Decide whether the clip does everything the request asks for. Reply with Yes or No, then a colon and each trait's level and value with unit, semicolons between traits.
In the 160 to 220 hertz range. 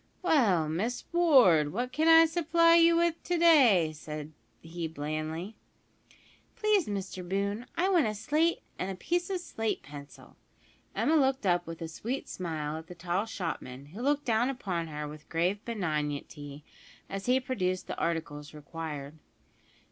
Yes: high, 190 Hz